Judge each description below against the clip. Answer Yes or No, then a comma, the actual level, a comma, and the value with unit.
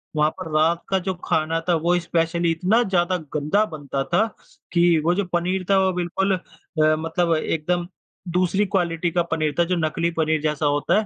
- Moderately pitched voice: Yes, medium, 170 Hz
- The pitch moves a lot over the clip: No, narrow, 2.4 semitones